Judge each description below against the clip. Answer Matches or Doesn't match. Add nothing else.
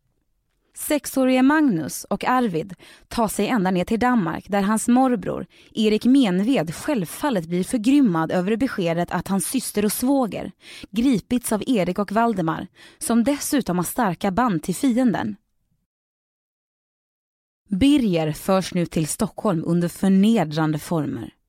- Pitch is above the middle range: Matches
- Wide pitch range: Matches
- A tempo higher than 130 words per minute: Doesn't match